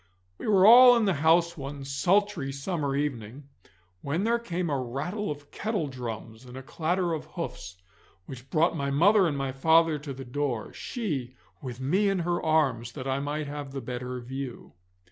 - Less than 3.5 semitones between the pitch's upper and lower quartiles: No, average, 4.7 semitones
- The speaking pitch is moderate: Yes, medium, 145 Hz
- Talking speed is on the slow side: No, average, 180 wpm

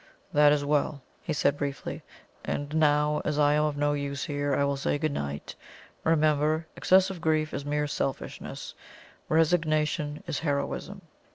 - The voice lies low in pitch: No, medium, 150 Hz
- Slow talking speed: No, average, 155 wpm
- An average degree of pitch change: No, narrow, 1.4 semitones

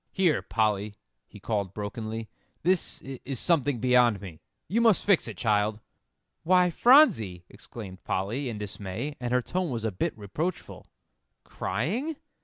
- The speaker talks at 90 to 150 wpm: Yes, average, 140 wpm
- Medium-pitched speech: No, low, 120 Hz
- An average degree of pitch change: No, wide, 7.8 semitones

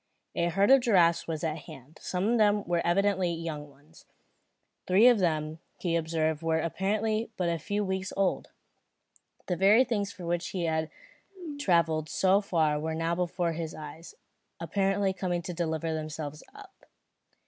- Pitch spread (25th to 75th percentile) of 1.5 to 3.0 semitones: No, average, 3.5 semitones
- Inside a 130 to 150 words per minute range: No, average, 160 wpm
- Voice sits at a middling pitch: Yes, medium, 170 Hz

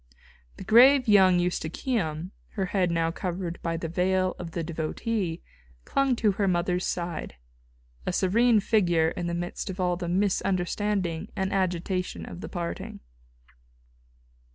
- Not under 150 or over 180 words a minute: No, average, 140 wpm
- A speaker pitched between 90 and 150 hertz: No, medium, 180 Hz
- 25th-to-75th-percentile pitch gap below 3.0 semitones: Yes, narrow, 2.5 semitones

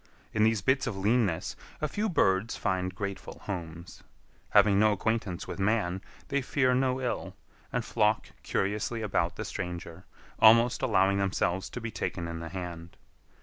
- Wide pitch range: No, average, 4.1 semitones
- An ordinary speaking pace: Yes, average, 155 wpm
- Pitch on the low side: Yes, low, 100 Hz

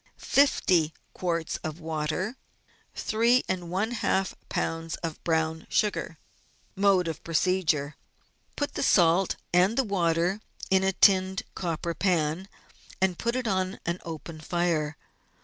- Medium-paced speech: No, slow, 120 wpm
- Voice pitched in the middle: Yes, medium, 175 Hz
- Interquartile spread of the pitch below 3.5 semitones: Yes, average, 2.9 semitones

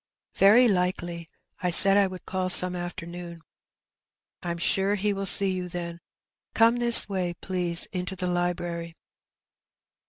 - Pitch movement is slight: Yes, narrow, 2.0 semitones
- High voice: No, medium, 180 Hz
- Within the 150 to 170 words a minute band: No, slow, 135 wpm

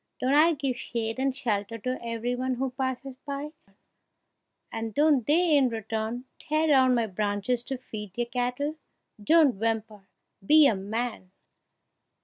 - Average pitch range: Yes, average, 3.8 semitones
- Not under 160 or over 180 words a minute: No, average, 145 wpm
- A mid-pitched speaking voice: No, high, 245 Hz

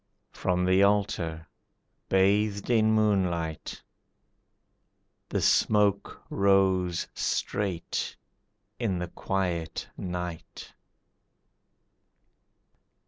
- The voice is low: Yes, very low, 95 Hz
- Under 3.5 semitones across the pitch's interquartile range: Yes, narrow, 2.4 semitones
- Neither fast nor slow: No, slow, 65 wpm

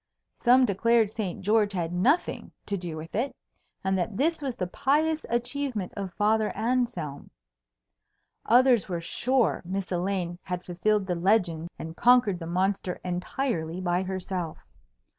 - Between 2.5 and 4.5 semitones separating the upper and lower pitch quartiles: No, average, 5.1 semitones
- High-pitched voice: Yes, high, 195 Hz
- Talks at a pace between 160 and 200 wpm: No, average, 140 wpm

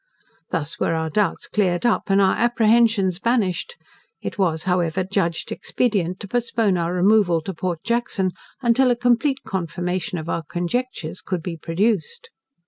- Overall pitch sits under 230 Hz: Yes, high, 190 Hz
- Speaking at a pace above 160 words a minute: No, average, 150 wpm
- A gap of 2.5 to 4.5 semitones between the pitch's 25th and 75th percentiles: No, average, 4.9 semitones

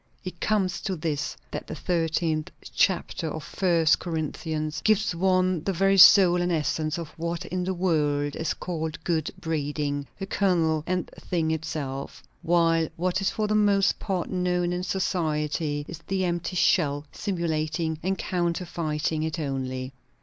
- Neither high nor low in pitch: Yes, medium, 165 Hz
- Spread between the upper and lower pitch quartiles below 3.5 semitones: Yes, average, 2.9 semitones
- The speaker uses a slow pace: No, average, 150 wpm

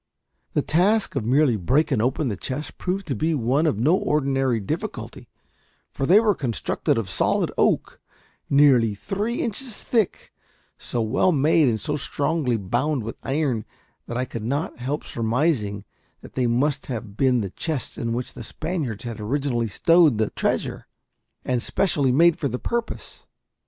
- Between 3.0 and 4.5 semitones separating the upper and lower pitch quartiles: No, average, 5.2 semitones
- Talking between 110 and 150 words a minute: No, average, 160 wpm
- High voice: No, low, 135 Hz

